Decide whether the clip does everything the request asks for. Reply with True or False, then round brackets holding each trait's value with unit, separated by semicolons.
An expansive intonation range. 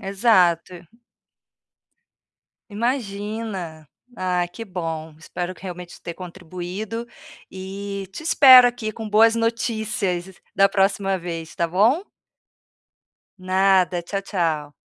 False (3.5 semitones)